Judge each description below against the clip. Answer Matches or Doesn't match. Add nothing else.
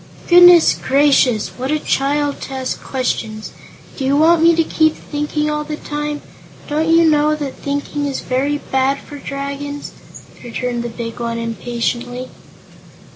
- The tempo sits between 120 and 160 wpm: Matches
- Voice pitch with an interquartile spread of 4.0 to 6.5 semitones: Doesn't match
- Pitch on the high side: Matches